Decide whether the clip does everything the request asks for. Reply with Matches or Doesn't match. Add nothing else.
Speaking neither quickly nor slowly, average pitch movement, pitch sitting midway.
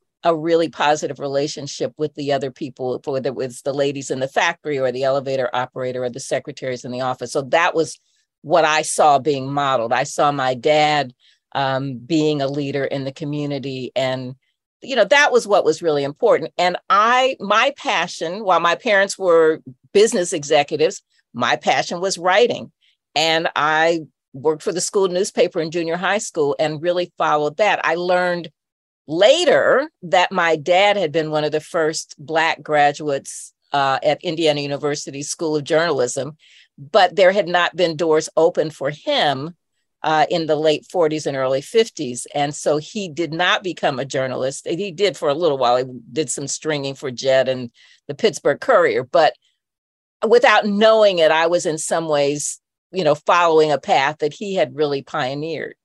Matches